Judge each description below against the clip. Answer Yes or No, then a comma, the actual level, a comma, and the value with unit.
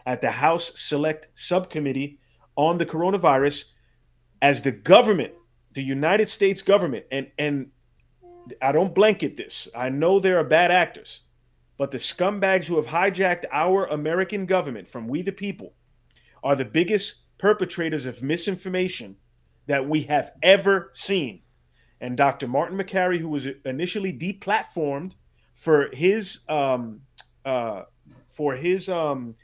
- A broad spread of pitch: Yes, wide, 5.7 semitones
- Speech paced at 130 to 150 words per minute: Yes, slow, 135 wpm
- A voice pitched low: No, medium, 155 Hz